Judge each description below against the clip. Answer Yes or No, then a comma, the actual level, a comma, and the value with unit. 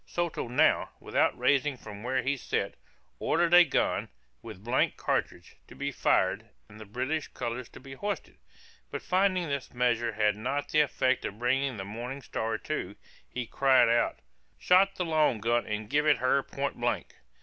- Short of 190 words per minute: Yes, average, 175 wpm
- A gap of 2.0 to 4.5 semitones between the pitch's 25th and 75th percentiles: Yes, average, 4.2 semitones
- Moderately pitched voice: No, low, 130 Hz